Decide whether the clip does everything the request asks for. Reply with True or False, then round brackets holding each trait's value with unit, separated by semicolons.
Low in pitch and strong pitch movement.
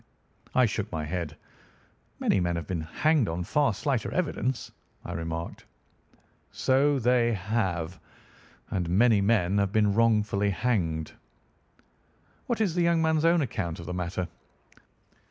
True (105 Hz; 6.6 semitones)